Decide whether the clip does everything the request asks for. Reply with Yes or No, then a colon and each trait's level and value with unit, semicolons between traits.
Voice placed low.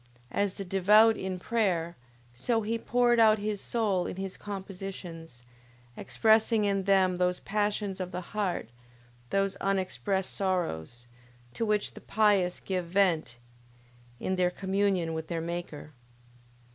No: high, 190 Hz